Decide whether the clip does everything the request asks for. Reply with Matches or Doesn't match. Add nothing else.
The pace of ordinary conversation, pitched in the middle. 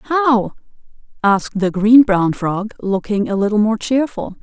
Doesn't match